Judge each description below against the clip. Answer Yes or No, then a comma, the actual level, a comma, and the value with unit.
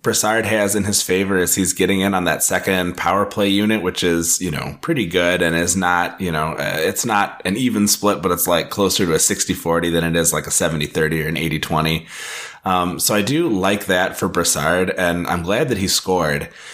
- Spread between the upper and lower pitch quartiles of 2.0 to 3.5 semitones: Yes, average, 3.2 semitones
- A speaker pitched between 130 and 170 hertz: No, very low, 90 Hz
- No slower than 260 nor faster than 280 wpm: No, fast, 220 wpm